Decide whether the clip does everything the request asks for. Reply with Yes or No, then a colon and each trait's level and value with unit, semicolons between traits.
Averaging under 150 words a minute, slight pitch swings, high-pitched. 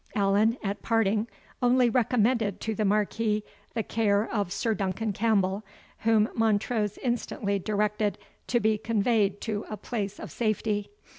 Yes: average, 140 wpm; narrow, 1.8 semitones; high, 215 Hz